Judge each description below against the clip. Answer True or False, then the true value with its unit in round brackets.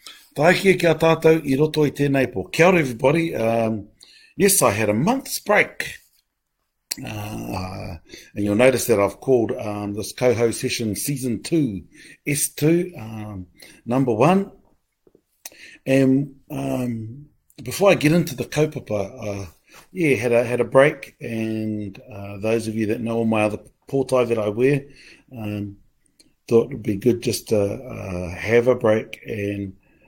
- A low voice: True (120 Hz)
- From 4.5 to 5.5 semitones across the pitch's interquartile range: True (5.0 semitones)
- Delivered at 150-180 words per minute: True (160 wpm)